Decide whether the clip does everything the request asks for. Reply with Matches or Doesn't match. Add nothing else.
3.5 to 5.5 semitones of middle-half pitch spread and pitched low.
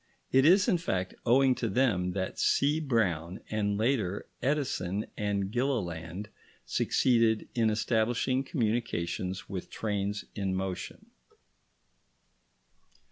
Matches